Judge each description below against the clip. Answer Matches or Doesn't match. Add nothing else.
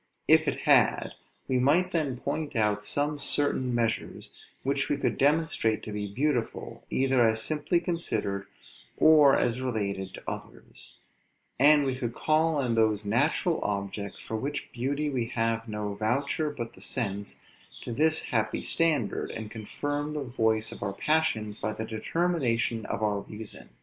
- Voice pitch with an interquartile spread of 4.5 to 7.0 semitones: Matches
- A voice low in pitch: Matches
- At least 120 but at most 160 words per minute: Matches